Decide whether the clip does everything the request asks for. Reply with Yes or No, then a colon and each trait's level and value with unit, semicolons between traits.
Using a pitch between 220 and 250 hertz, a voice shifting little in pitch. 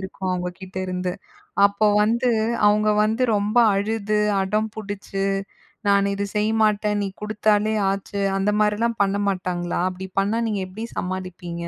No: high, 200 Hz; narrow, 2.1 semitones